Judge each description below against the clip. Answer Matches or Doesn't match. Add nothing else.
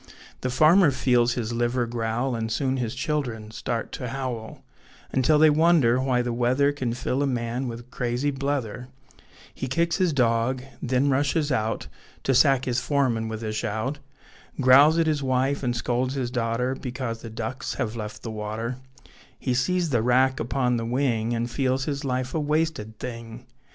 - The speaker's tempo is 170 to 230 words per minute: Matches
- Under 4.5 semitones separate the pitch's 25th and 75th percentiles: Matches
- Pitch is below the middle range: Matches